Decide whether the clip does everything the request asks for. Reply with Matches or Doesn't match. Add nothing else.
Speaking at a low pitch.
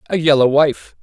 Doesn't match